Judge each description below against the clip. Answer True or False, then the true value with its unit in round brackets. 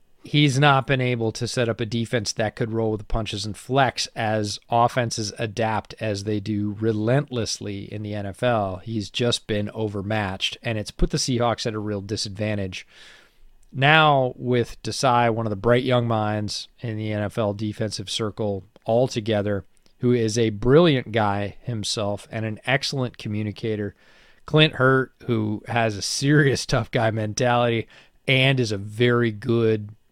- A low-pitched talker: True (115 Hz)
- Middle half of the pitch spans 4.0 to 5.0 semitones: False (2.7 semitones)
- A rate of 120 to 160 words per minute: True (155 wpm)